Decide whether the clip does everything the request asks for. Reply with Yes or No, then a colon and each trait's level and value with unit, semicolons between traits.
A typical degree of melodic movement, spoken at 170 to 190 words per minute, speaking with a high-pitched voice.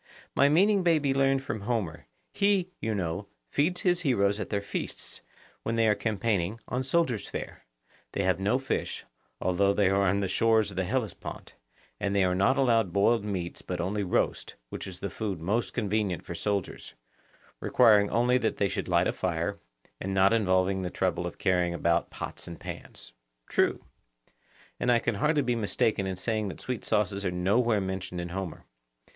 No: average, 4.1 semitones; average, 185 wpm; low, 100 Hz